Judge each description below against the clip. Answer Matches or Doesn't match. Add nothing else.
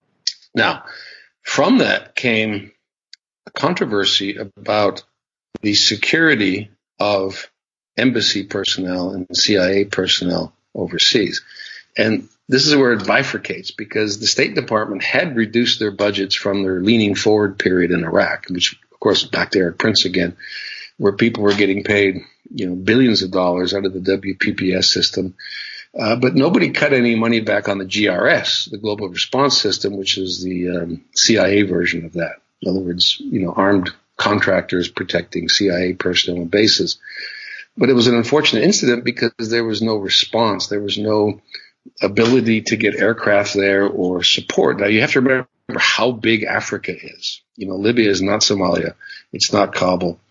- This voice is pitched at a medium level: Doesn't match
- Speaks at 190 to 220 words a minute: Doesn't match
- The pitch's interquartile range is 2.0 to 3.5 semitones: Matches